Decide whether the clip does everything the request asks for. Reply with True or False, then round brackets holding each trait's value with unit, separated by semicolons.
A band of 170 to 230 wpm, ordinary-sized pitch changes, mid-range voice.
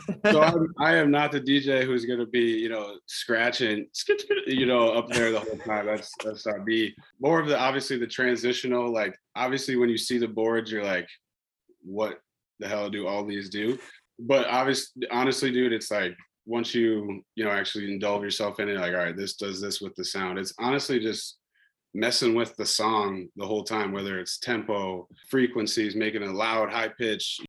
False (195 wpm; 4.0 semitones; 115 Hz)